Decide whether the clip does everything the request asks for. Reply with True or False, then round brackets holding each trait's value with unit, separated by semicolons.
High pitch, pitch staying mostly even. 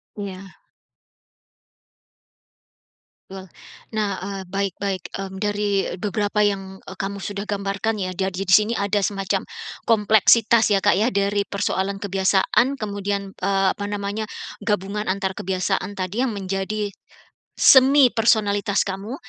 True (200 Hz; 1.4 semitones)